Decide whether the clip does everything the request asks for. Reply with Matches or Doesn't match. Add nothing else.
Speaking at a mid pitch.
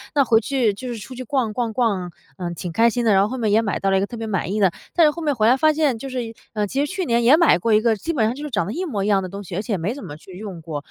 Doesn't match